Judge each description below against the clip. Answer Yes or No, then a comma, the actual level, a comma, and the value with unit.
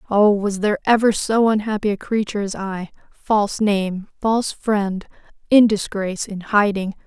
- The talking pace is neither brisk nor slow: Yes, average, 155 wpm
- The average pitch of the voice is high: Yes, high, 205 Hz